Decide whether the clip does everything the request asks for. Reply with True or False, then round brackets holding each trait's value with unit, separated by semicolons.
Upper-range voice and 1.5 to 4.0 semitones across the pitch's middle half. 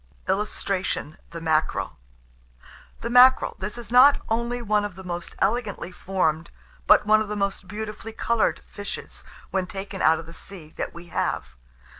True (200 Hz; 3.6 semitones)